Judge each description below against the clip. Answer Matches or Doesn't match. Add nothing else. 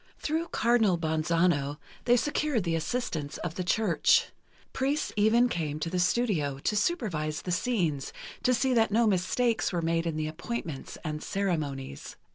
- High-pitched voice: Doesn't match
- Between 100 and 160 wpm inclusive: Matches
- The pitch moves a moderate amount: Doesn't match